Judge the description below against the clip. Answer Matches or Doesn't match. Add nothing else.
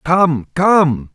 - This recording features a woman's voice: Doesn't match